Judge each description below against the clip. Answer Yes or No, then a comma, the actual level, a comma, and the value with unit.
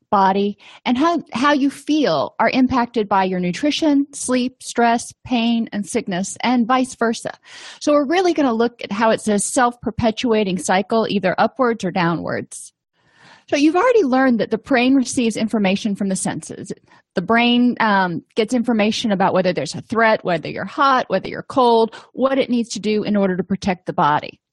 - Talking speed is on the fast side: No, average, 185 wpm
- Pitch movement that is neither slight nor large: Yes, average, 4.2 semitones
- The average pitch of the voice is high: Yes, high, 230 Hz